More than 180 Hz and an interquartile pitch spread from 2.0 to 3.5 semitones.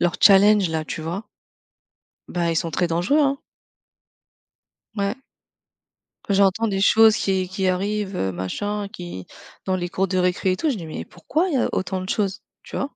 Yes: high, 190 Hz; average, 2.9 semitones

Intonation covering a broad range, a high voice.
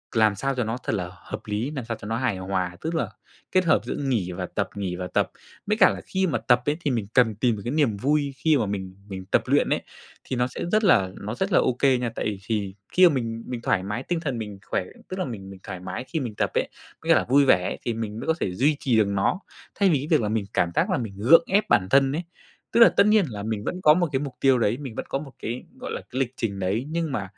No: wide, 6.1 semitones; low, 120 Hz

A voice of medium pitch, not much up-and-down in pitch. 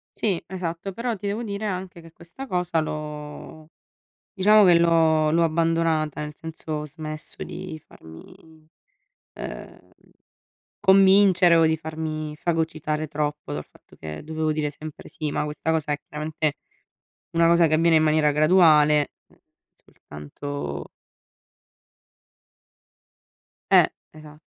Yes: medium, 160 Hz; narrow, 2.1 semitones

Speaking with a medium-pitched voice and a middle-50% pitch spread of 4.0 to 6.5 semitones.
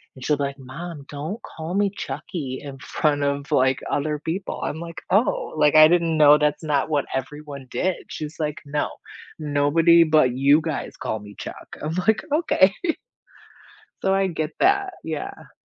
No: medium, 150 Hz; average, 2.8 semitones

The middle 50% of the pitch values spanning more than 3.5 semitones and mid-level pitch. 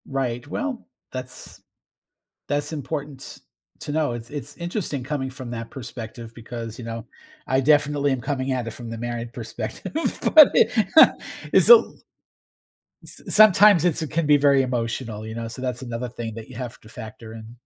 No: average, 4.0 semitones; low, 130 Hz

